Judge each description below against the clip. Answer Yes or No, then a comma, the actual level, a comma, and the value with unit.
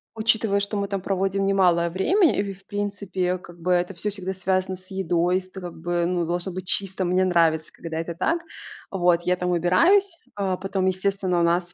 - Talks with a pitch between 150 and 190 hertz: Yes, medium, 185 Hz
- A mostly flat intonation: Yes, narrow, 2.0 semitones